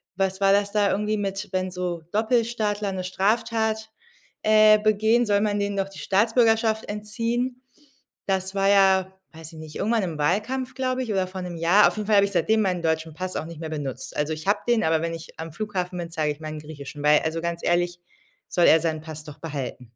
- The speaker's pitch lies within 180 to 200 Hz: Yes, high, 190 Hz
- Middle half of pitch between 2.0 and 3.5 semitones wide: No, average, 4.6 semitones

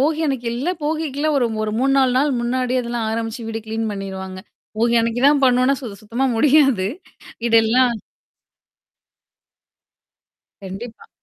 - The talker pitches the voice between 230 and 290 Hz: Yes, high, 240 Hz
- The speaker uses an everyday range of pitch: Yes, average, 3.3 semitones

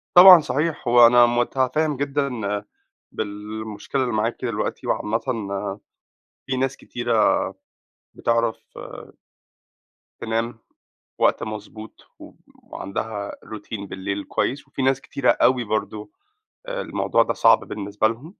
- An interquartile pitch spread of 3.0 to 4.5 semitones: Yes, average, 3.7 semitones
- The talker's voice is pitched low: Yes, low, 115 Hz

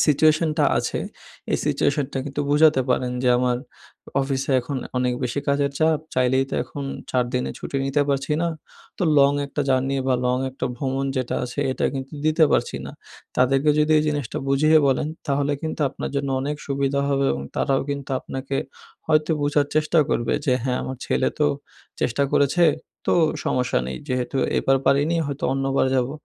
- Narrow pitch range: Yes, narrow, 2.0 semitones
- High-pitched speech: No, medium, 140 Hz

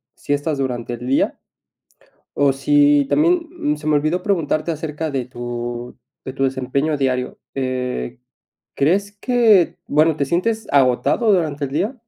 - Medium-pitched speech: Yes, medium, 145 Hz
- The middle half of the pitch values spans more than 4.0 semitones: Yes, average, 4.6 semitones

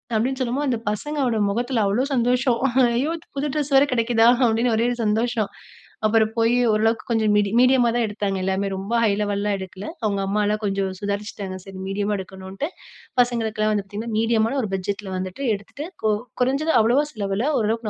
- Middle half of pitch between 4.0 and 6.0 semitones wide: No, average, 3.2 semitones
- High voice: Yes, high, 220 Hz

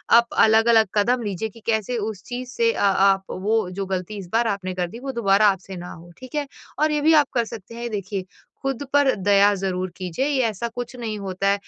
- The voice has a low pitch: No, high, 215 Hz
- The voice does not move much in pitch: No, average, 3.9 semitones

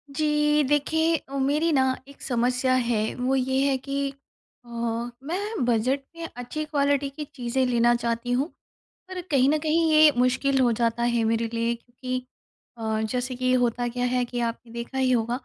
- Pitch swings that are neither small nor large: Yes, average, 3.1 semitones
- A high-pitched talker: Yes, very high, 255 Hz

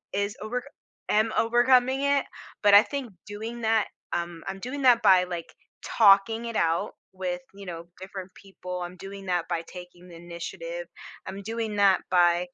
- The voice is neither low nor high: No, high, 195 Hz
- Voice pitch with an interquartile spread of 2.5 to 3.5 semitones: No, average, 4.3 semitones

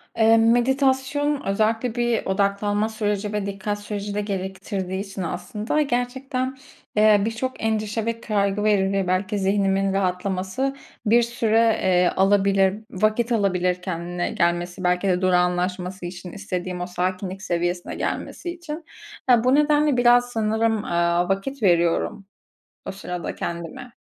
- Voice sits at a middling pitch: No, high, 205 Hz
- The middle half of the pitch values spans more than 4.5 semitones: No, average, 3.8 semitones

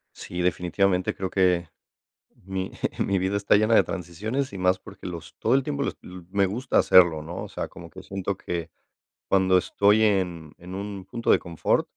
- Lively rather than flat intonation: No, narrow, 2.4 semitones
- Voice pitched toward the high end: No, very low, 95 Hz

